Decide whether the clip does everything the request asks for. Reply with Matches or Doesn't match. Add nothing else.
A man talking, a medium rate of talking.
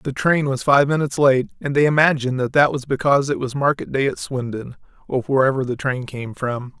Doesn't match